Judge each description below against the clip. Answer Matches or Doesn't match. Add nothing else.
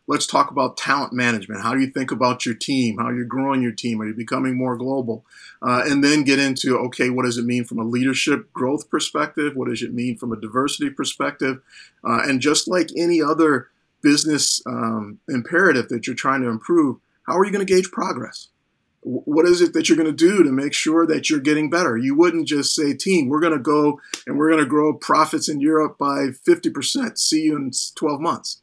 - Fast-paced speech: Matches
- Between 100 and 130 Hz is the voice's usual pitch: Doesn't match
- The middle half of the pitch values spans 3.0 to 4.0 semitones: Doesn't match